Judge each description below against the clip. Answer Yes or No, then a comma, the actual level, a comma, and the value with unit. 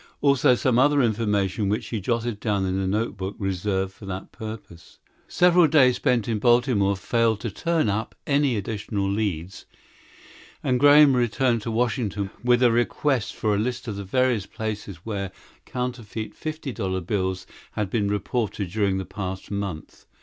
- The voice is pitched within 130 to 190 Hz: No, low, 110 Hz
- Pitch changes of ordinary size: Yes, average, 3.9 semitones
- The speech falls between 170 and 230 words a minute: No, average, 160 wpm